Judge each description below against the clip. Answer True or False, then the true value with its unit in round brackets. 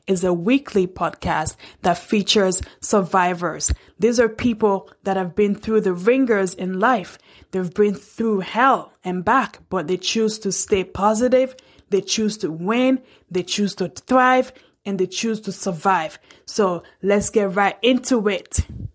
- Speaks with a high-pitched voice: True (200 Hz)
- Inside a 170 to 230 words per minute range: False (155 wpm)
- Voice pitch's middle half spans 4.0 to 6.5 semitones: False (3.3 semitones)